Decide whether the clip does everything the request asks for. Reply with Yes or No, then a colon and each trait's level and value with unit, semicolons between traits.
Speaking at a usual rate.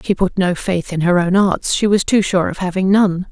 No: fast, 270 wpm